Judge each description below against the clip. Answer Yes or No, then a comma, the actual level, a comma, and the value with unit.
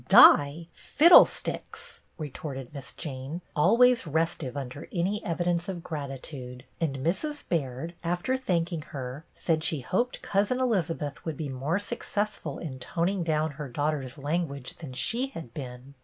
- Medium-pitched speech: Yes, medium, 155 Hz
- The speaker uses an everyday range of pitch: Yes, average, 4.3 semitones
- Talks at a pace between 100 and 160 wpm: Yes, average, 145 wpm